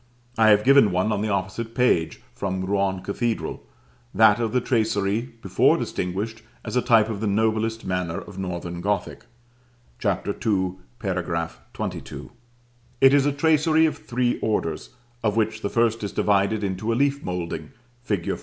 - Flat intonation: No, average, 3.5 semitones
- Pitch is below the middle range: Yes, low, 105 Hz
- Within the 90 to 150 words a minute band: No, average, 160 wpm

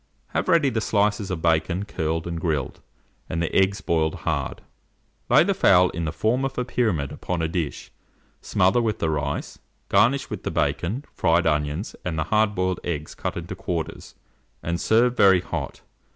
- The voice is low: Yes, very low, 90 Hz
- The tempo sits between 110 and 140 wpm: No, average, 180 wpm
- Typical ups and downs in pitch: Yes, average, 4.9 semitones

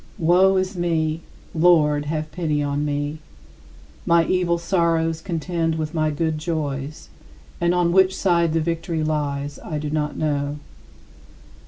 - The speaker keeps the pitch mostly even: Yes, narrow, 2.3 semitones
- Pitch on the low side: No, medium, 160 Hz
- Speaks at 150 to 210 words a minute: No, average, 140 wpm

